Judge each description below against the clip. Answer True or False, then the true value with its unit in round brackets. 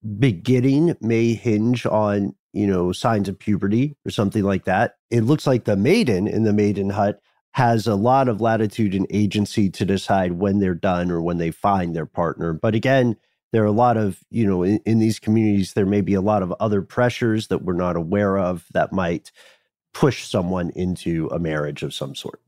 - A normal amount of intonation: True (3.2 semitones)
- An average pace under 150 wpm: False (205 wpm)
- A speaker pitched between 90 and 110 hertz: True (105 Hz)